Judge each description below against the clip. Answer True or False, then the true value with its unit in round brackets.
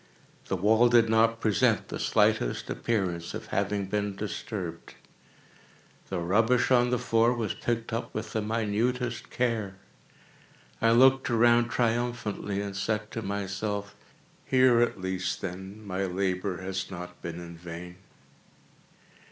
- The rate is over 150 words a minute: False (135 wpm)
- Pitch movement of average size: True (3.5 semitones)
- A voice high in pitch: False (105 Hz)